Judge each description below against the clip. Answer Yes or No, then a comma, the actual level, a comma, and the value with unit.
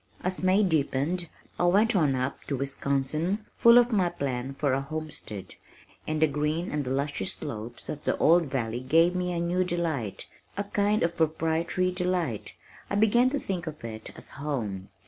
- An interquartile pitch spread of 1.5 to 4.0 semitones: No, average, 4.9 semitones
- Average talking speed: Yes, average, 175 wpm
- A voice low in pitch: No, medium, 160 Hz